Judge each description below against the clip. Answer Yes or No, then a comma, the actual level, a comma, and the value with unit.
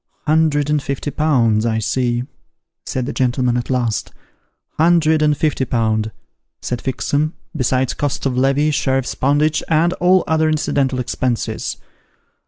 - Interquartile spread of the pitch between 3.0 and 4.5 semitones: Yes, average, 3.7 semitones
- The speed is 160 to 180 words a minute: No, average, 150 wpm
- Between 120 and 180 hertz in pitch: Yes, low, 135 Hz